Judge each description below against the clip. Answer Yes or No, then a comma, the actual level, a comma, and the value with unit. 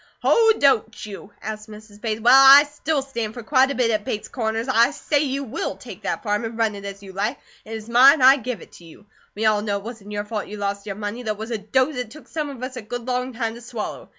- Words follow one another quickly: Yes, fast, 280 wpm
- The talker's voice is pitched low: No, high, 225 Hz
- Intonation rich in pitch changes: No, average, 3.7 semitones